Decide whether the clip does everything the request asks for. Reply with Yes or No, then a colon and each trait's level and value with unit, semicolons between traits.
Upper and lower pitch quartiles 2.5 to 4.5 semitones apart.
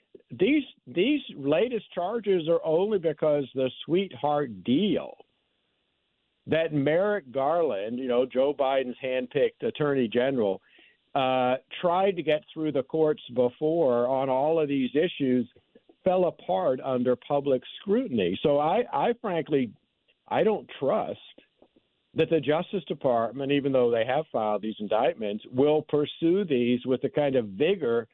No: average, 5.1 semitones